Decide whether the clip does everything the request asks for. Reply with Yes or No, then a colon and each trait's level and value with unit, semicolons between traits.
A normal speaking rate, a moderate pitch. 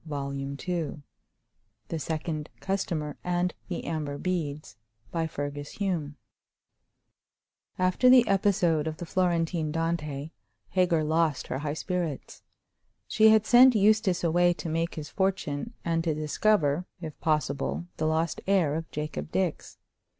No: slow, 120 wpm; medium, 165 Hz